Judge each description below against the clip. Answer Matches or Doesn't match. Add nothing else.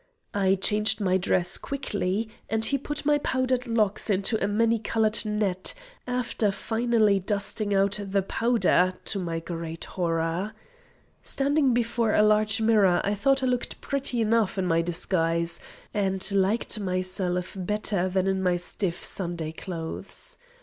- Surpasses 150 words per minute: Doesn't match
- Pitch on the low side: Doesn't match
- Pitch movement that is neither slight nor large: Matches